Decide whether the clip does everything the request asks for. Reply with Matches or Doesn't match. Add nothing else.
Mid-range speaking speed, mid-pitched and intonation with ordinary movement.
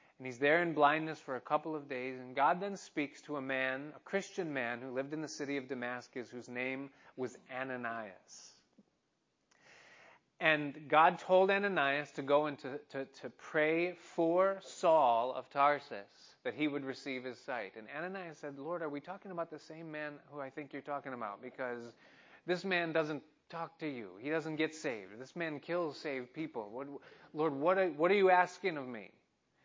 Matches